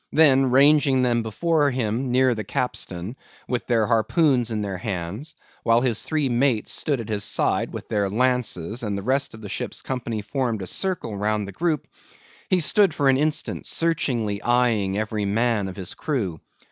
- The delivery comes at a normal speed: Yes, average, 180 wpm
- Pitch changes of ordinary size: Yes, average, 4.4 semitones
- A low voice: Yes, low, 120 Hz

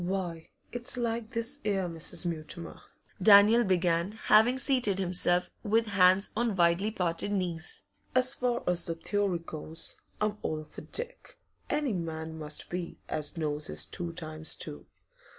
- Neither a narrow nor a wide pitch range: Yes, average, 4.7 semitones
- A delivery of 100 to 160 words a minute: Yes, average, 150 wpm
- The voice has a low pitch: No, medium, 185 Hz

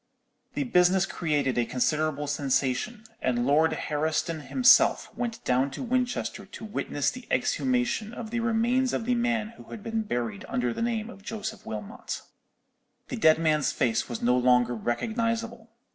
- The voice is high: No, medium, 180 Hz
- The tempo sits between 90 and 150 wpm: No, average, 160 wpm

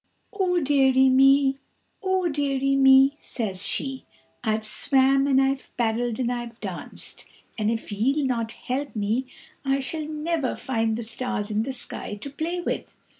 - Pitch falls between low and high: No, very high, 265 Hz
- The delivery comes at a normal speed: Yes, average, 155 wpm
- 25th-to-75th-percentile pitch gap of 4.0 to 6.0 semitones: No, average, 3.2 semitones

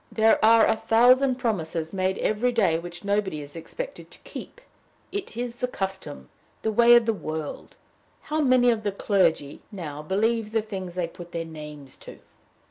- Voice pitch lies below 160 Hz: No, high, 205 Hz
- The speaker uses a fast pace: No, average, 175 wpm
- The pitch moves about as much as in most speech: No, wide, 5.8 semitones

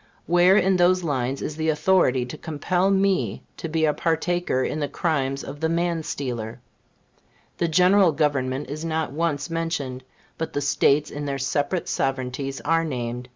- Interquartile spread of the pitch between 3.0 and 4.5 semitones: Yes, average, 3.9 semitones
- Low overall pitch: No, medium, 150 Hz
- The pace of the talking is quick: No, average, 165 wpm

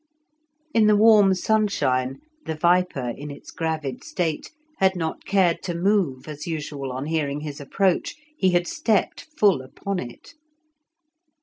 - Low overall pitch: No, medium, 165 Hz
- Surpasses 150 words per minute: No, average, 140 wpm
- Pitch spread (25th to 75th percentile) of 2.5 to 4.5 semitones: No, average, 5.3 semitones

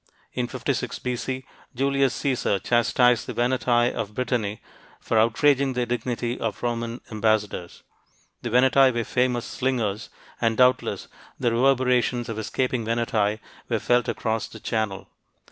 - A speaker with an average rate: No, slow, 130 wpm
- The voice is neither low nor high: No, low, 120 Hz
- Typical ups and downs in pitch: No, narrow, 2.2 semitones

